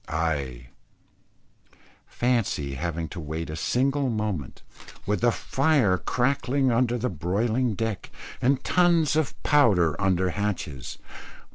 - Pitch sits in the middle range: No, low, 105 Hz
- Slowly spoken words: Yes, slow, 125 wpm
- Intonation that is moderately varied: No, wide, 7.4 semitones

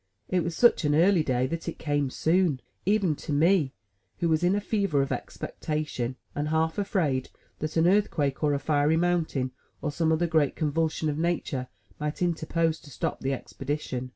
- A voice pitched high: No, medium, 155 Hz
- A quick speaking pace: No, average, 180 wpm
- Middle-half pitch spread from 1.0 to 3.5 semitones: Yes, average, 3.0 semitones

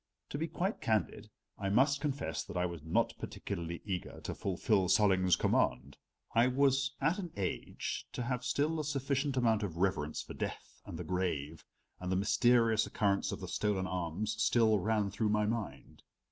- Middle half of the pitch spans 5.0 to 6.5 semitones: Yes, wide, 5.6 semitones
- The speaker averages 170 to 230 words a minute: Yes, average, 175 wpm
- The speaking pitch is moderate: No, low, 105 Hz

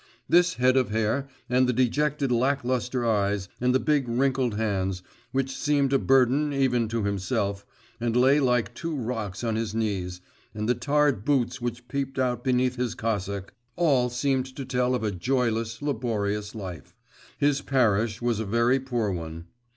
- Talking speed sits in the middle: Yes, average, 170 wpm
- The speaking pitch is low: Yes, low, 125 Hz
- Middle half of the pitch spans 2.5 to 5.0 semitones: Yes, average, 3.6 semitones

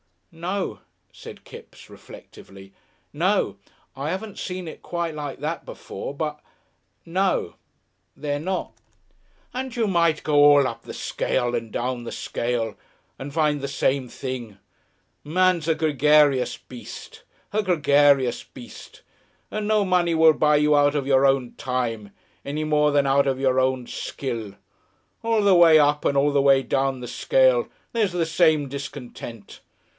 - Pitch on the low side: No, medium, 145 Hz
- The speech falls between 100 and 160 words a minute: Yes, average, 150 wpm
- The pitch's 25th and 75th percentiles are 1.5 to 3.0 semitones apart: No, average, 4.2 semitones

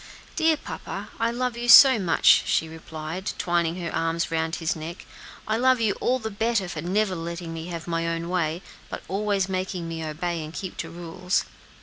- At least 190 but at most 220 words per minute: Yes, average, 195 wpm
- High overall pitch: No, medium, 175 Hz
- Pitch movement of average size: Yes, average, 4.0 semitones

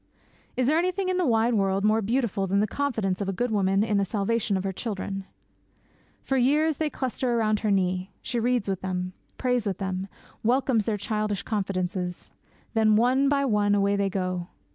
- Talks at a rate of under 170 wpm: No, average, 190 wpm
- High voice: Yes, high, 210 Hz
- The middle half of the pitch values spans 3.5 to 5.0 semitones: Yes, average, 4.1 semitones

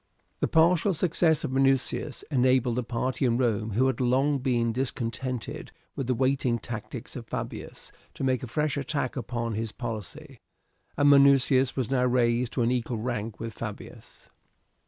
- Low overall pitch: Yes, low, 125 Hz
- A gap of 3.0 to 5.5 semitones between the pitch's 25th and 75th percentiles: No, narrow, 2.5 semitones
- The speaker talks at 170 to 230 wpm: No, average, 160 wpm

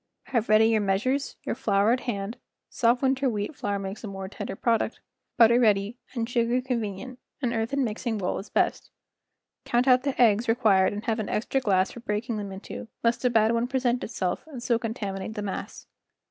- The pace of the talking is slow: No, average, 200 wpm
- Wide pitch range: No, average, 3.1 semitones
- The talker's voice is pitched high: Yes, high, 230 Hz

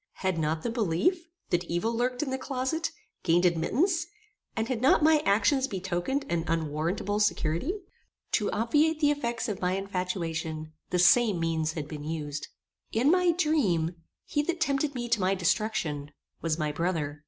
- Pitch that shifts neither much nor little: No, wide, 8.2 semitones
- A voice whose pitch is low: No, high, 195 Hz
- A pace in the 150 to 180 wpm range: Yes, average, 165 wpm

